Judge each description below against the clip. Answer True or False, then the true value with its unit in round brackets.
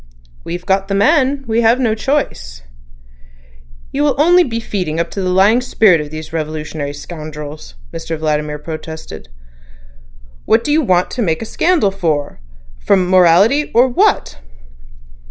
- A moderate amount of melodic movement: False (7.4 semitones)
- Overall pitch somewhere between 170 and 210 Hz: True (185 Hz)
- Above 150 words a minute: False (135 wpm)